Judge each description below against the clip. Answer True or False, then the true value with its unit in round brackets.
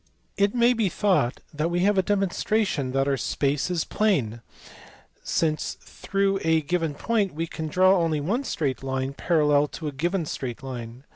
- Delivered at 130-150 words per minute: False (170 wpm)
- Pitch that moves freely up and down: True (5.9 semitones)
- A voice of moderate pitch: True (160 Hz)